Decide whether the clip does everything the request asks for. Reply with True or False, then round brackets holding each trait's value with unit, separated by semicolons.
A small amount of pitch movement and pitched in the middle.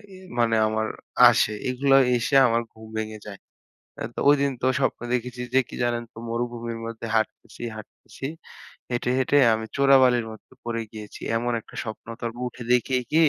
False (2.2 semitones; 120 Hz)